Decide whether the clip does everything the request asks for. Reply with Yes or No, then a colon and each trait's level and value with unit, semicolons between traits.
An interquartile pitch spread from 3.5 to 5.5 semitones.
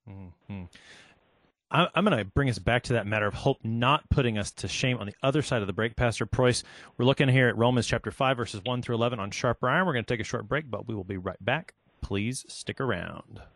Yes: average, 3.8 semitones